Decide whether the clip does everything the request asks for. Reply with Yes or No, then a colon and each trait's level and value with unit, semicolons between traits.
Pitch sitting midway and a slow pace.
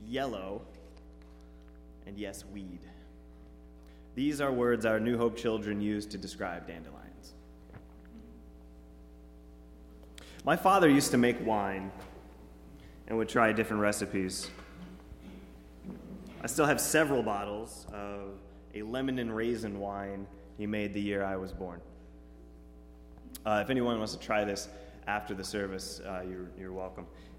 No: very low, 95 Hz; slow, 125 wpm